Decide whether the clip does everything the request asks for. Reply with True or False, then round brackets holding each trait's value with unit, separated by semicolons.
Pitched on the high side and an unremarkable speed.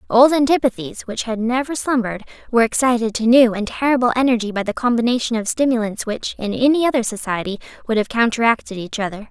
True (235 Hz; 180 wpm)